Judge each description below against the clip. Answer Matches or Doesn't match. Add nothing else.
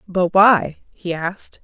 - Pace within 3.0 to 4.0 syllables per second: Matches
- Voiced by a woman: Matches